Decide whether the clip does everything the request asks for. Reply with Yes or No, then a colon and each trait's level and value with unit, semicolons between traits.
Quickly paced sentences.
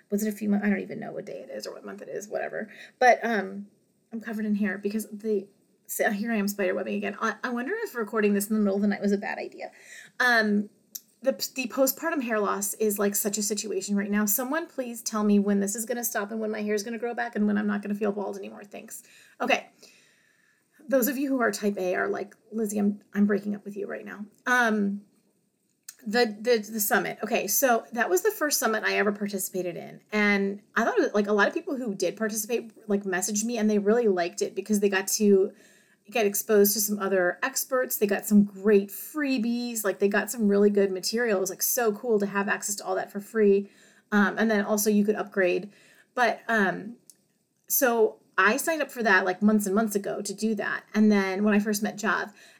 Yes: fast, 245 wpm